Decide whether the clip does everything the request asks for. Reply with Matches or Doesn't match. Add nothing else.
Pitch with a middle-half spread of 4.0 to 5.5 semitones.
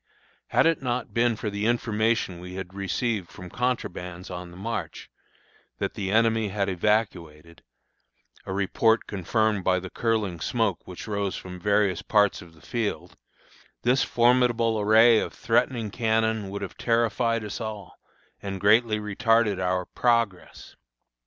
Doesn't match